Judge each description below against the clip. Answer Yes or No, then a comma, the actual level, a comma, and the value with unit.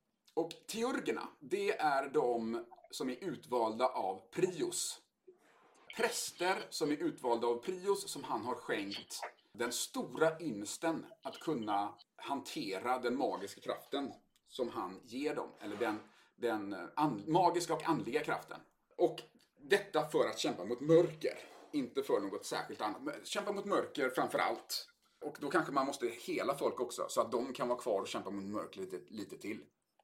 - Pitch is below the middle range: No, high, 200 Hz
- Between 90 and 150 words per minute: No, average, 160 wpm